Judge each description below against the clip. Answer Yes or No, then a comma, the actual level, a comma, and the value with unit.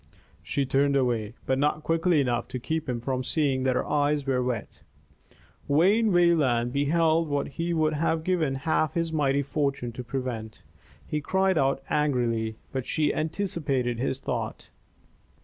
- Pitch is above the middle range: No, medium, 140 Hz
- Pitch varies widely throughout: No, average, 3.8 semitones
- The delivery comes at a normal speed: Yes, average, 155 wpm